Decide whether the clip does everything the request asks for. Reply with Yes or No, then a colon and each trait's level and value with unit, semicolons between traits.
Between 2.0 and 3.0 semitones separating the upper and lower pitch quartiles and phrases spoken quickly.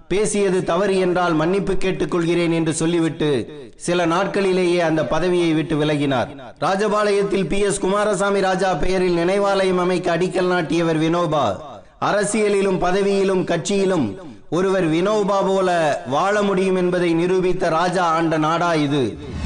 No: narrow, 2.4 semitones; average, 115 wpm